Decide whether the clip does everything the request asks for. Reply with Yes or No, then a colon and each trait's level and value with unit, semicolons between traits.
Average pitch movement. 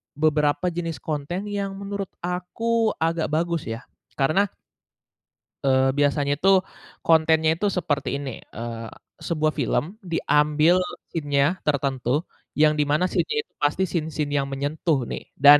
Yes: average, 3.3 semitones